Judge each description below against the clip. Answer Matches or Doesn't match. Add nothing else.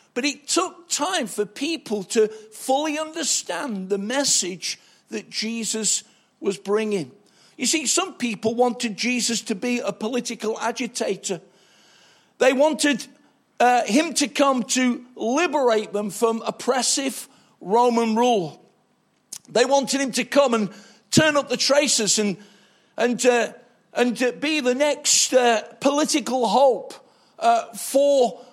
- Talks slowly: Matches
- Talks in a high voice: Matches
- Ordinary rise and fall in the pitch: Matches